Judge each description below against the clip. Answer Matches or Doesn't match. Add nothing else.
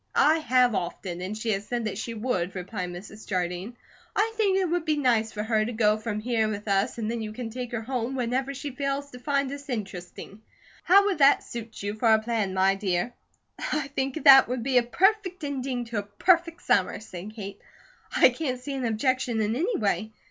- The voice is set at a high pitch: Matches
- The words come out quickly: Matches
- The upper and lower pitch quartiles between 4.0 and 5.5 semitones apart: Matches